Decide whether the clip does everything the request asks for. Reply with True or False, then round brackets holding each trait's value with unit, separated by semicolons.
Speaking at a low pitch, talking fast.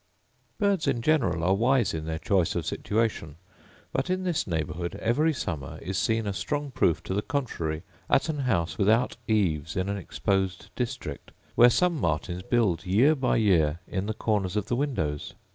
False (105 Hz; 180 wpm)